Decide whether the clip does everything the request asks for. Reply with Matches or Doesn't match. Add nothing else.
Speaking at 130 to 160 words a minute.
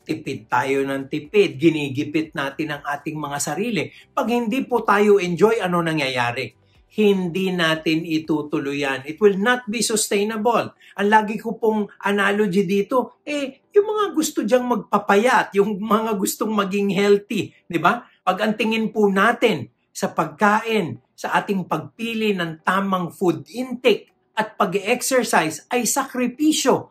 Matches